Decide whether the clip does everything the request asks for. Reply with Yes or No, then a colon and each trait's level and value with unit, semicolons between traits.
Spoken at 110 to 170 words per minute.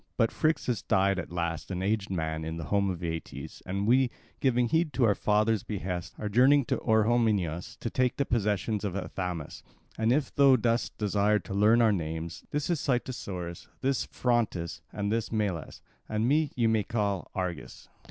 No: average, 180 wpm